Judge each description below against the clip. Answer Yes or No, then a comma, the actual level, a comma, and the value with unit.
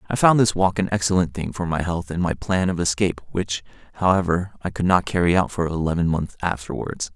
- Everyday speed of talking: No, fast, 220 wpm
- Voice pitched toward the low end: Yes, very low, 90 Hz